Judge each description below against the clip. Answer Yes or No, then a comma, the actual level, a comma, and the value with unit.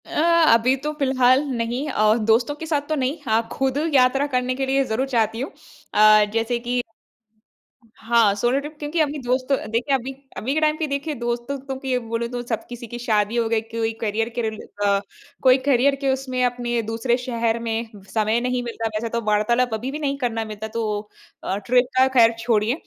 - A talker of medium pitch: No, high, 240 Hz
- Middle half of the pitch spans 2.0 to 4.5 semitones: Yes, average, 2.9 semitones